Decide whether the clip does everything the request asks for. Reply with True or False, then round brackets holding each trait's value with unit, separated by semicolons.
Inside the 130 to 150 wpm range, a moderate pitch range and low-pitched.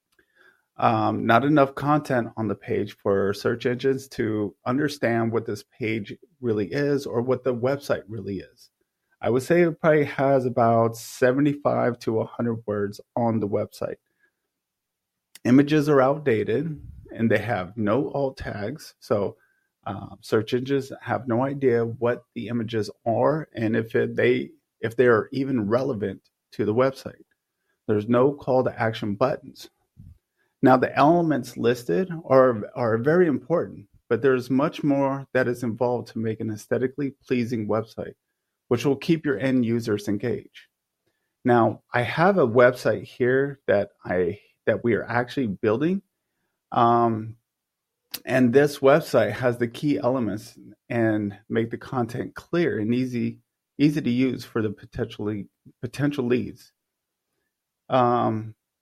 True (145 wpm; 3.4 semitones; 125 Hz)